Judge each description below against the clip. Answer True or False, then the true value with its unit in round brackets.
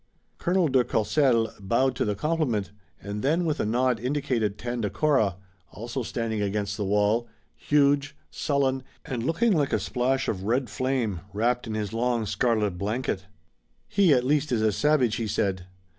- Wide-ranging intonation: False (4.6 semitones)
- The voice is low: True (120 Hz)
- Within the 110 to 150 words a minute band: False (160 wpm)